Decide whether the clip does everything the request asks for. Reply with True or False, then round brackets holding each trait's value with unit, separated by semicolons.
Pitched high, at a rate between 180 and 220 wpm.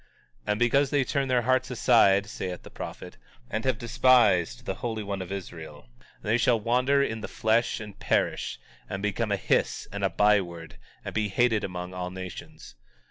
False (105 Hz; 185 wpm)